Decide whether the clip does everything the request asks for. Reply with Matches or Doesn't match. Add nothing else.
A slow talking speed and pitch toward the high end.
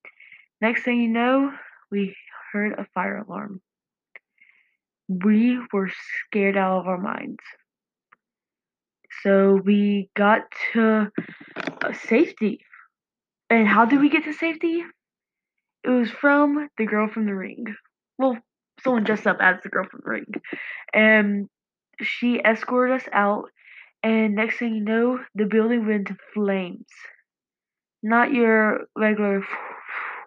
Matches